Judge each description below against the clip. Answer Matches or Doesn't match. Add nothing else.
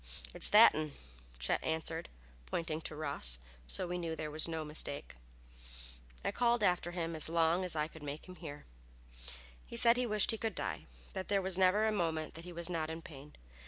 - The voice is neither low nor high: Matches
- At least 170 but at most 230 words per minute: Matches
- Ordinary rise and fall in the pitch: Matches